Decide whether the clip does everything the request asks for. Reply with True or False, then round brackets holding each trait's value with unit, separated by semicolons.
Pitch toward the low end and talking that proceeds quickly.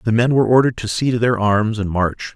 True (115 Hz; 280 wpm)